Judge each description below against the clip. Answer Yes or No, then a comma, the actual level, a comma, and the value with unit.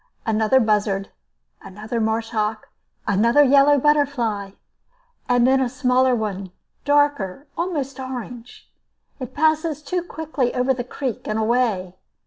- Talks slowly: Yes, slow, 120 wpm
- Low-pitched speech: No, very high, 250 Hz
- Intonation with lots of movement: No, average, 4.7 semitones